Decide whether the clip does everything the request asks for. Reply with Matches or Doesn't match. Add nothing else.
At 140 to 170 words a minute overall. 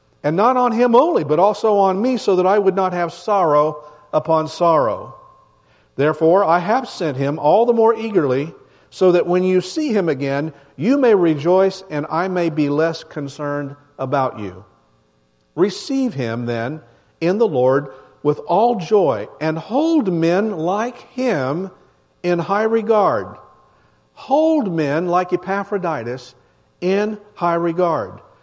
Matches